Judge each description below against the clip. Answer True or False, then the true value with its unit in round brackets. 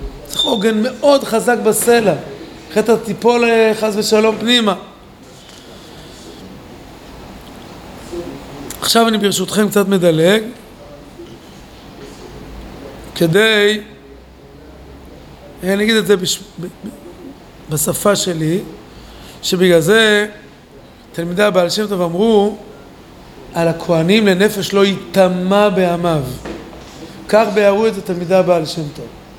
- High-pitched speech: True (200 Hz)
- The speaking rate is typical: False (85 wpm)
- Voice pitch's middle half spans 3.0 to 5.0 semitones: True (4.0 semitones)